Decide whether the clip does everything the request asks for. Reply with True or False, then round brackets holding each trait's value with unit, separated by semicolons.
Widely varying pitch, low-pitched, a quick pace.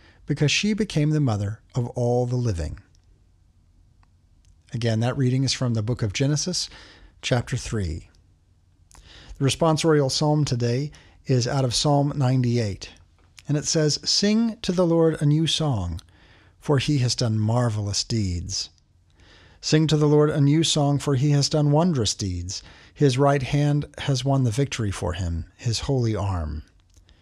False (8.0 semitones; 120 Hz; 155 wpm)